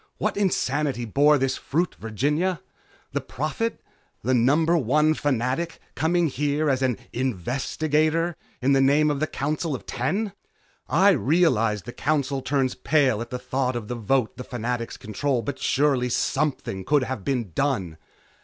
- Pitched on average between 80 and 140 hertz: Yes, low, 135 Hz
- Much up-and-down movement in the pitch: No, average, 3.7 semitones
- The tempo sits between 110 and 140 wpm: No, average, 155 wpm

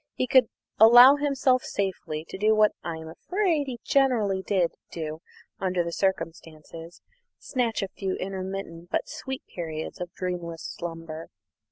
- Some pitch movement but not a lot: No, wide, 6.5 semitones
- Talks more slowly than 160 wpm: Yes, average, 145 wpm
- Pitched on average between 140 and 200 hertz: Yes, high, 190 Hz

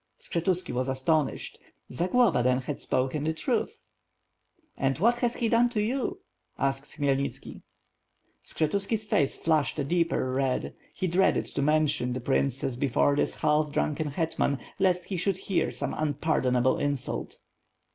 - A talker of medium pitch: Yes, medium, 150 Hz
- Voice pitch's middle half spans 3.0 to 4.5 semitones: No, average, 5.2 semitones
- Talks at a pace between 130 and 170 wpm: Yes, average, 140 wpm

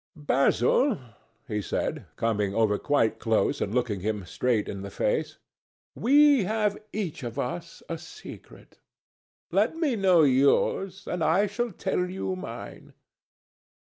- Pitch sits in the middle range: Yes, medium, 160 Hz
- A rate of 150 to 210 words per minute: No, slow, 135 wpm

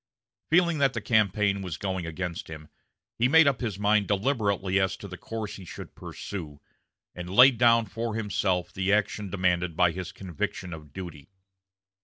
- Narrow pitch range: No, average, 3.8 semitones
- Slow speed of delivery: No, average, 170 wpm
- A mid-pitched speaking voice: No, low, 100 Hz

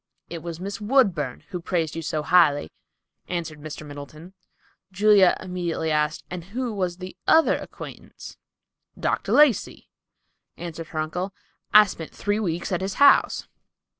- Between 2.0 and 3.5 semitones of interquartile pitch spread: No, average, 3.9 semitones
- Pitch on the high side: No, medium, 175 Hz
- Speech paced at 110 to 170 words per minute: Yes, average, 140 wpm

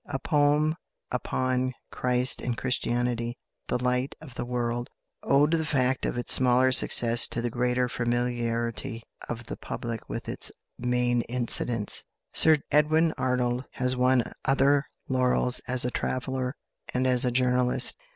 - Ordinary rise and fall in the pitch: No, narrow, 1.2 semitones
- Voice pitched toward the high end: No, low, 125 Hz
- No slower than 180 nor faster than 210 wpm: No, average, 140 wpm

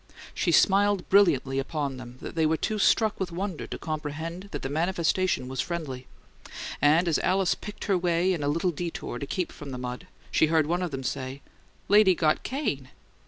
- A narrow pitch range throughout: No, average, 4.8 semitones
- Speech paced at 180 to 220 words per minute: Yes, average, 195 wpm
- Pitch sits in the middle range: Yes, medium, 165 Hz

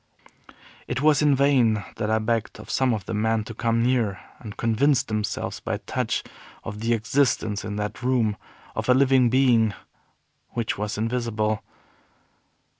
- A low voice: Yes, low, 115 Hz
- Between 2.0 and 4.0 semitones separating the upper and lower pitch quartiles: Yes, average, 3.0 semitones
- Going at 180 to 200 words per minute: No, average, 155 wpm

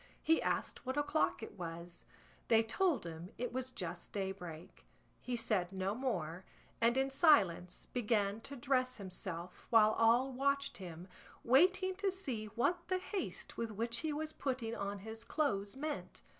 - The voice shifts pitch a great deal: Yes, wide, 6.0 semitones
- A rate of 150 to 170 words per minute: Yes, average, 155 wpm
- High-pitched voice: Yes, high, 230 Hz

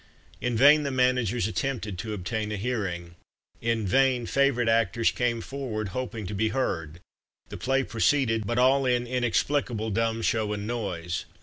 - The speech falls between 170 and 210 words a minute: No, average, 160 wpm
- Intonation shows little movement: No, average, 3.2 semitones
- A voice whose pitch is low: Yes, low, 115 Hz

